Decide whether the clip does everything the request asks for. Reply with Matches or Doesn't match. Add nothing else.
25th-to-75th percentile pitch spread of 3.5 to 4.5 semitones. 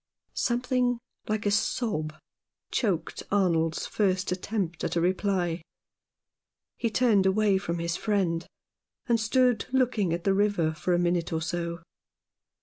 Matches